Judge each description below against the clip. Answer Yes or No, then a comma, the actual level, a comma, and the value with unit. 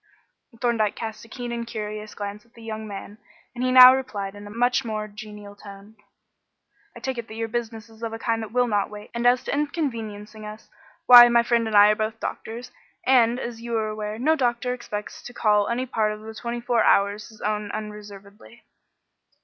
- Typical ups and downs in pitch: No, narrow, 2.2 semitones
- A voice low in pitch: No, high, 225 Hz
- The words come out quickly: Yes, fast, 215 wpm